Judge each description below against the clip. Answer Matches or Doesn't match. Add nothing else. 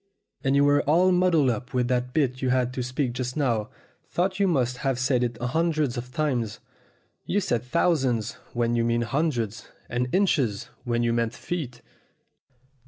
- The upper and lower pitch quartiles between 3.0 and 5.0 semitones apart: Matches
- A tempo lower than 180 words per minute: Matches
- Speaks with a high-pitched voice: Doesn't match